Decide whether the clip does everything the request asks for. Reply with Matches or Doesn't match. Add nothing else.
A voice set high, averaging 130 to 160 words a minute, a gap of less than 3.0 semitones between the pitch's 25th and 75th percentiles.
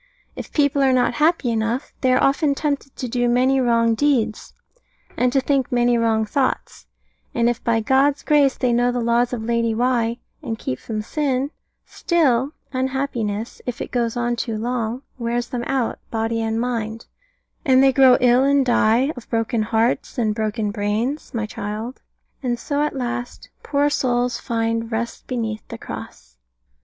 Doesn't match